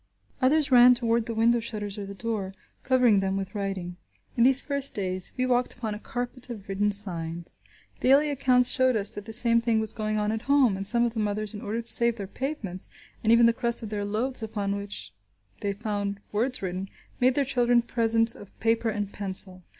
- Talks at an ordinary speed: No, fast, 210 wpm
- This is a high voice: Yes, high, 225 Hz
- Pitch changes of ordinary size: Yes, average, 3.2 semitones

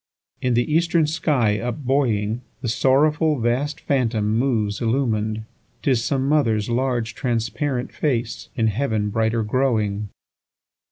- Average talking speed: No, slow, 105 wpm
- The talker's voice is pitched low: Yes, low, 120 Hz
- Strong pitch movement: No, average, 3.7 semitones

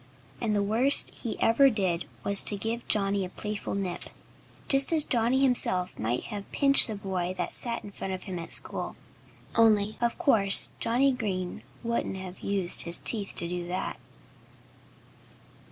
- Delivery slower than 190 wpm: Yes, average, 165 wpm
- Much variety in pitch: No, average, 3.8 semitones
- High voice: Yes, high, 205 Hz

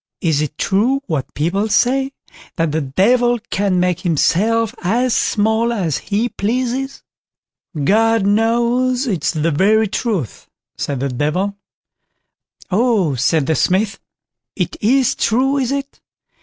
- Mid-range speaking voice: No, high, 210 Hz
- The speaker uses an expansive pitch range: Yes, wide, 6.3 semitones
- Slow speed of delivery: Yes, slow, 130 wpm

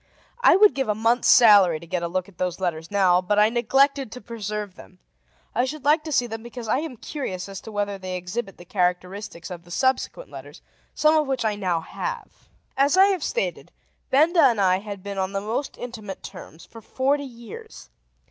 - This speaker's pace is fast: Yes, fast, 210 wpm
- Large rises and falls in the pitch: Yes, wide, 6.2 semitones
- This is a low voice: No, high, 215 Hz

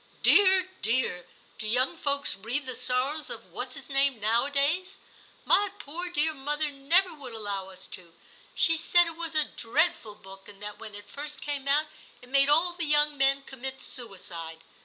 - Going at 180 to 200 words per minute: Yes, average, 185 wpm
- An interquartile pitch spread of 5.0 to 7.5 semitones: Yes, wide, 5.4 semitones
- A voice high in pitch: Yes, very high, 275 Hz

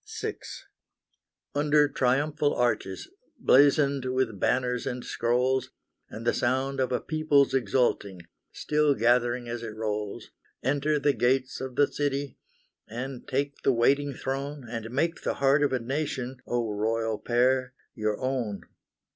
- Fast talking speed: No, average, 140 wpm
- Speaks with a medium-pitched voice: No, low, 130 Hz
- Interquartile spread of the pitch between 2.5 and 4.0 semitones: Yes, average, 2.8 semitones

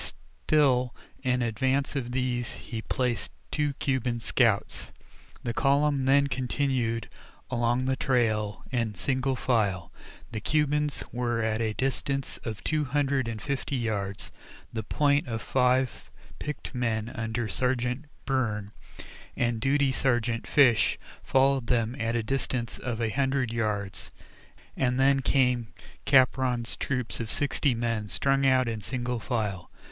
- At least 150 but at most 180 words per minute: No, slow, 135 wpm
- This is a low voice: Yes, low, 125 Hz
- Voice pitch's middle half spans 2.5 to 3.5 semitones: Yes, average, 2.8 semitones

